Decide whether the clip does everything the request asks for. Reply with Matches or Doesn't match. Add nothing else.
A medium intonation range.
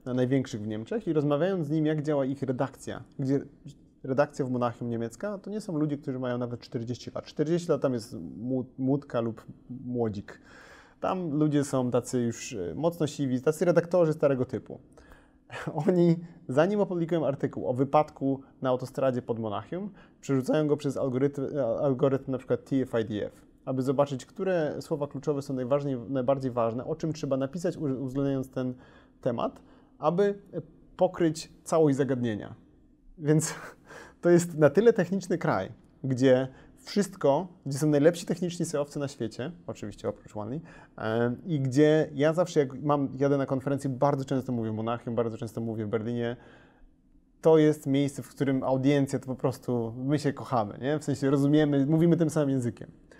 Matches